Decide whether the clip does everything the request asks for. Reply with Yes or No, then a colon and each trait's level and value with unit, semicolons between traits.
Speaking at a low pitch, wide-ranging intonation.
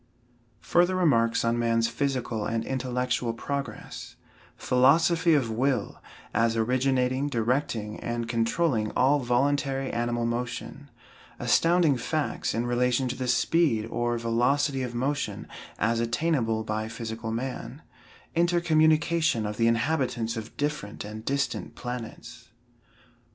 No: low, 125 Hz; average, 3.5 semitones